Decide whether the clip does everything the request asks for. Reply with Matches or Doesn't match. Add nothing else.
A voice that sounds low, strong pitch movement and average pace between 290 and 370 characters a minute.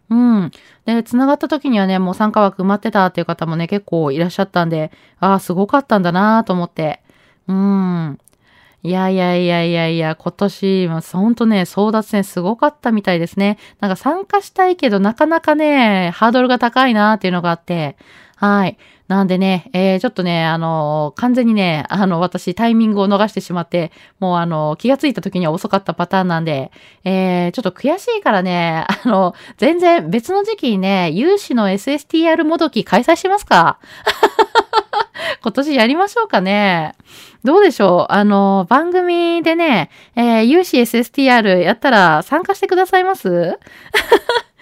Doesn't match